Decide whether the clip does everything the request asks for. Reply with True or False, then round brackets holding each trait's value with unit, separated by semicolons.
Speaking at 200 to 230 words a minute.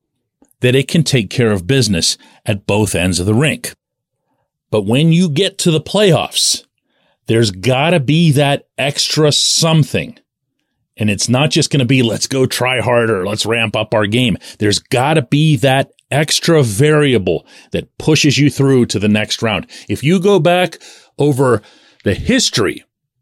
False (160 wpm)